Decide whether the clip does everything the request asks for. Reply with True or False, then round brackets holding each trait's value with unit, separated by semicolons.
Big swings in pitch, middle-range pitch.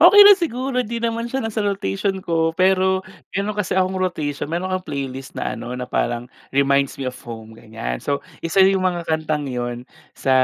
True (6.7 semitones; 170 Hz)